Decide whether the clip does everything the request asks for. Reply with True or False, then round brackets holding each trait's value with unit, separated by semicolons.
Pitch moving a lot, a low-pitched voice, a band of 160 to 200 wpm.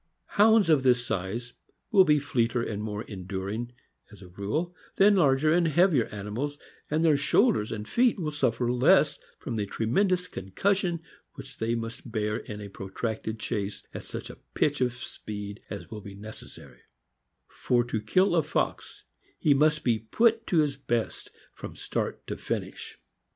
True (6.9 semitones; 125 Hz; 170 wpm)